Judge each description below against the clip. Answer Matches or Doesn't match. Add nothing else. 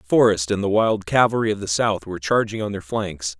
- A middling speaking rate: Doesn't match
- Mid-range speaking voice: Doesn't match